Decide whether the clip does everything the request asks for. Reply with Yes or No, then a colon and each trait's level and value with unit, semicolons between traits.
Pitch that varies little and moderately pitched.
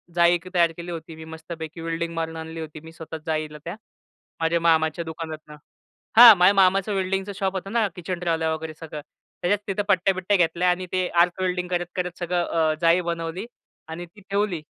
Yes: narrow, 2.2 semitones; medium, 170 Hz